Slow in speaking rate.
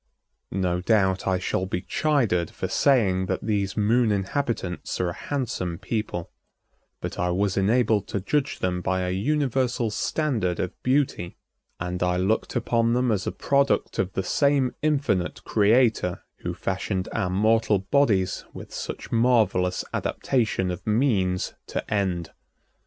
No: average, 145 wpm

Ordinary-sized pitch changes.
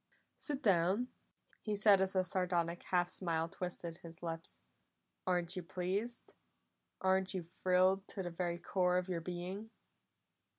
No: narrow, 1.7 semitones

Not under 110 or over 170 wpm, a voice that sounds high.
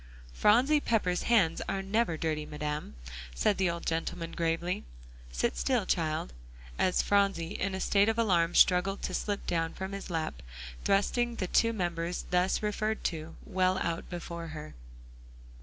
No: average, 155 wpm; medium, 180 Hz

